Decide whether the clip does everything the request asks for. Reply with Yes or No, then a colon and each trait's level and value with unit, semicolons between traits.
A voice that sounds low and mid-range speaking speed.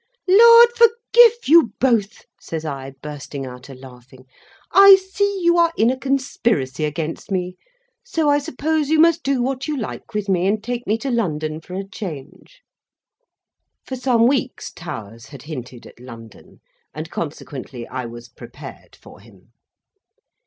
No: high, 205 Hz; average, 155 wpm